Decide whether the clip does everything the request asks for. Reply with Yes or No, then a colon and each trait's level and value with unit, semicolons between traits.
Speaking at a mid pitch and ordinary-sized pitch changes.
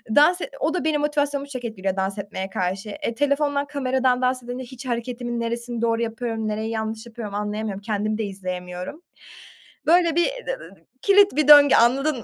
No: high, 240 Hz; average, 4.9 semitones